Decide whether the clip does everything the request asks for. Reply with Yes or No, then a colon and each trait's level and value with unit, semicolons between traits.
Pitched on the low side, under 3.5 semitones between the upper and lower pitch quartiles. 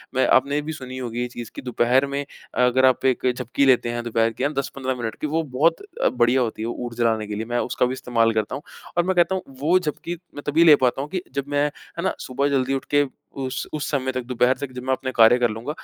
Yes: low, 130 Hz; average, 2.9 semitones